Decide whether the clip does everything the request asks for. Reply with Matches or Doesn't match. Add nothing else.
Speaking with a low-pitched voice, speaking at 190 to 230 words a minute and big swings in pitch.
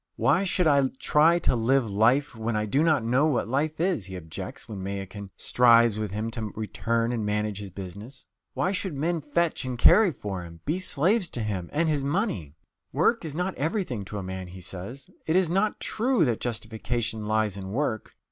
Matches